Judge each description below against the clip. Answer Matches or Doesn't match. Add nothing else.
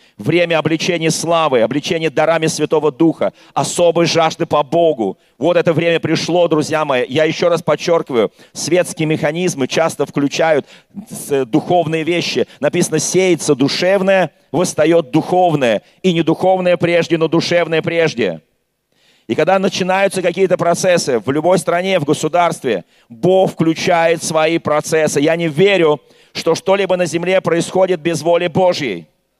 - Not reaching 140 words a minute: Matches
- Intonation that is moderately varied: Doesn't match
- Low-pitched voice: Doesn't match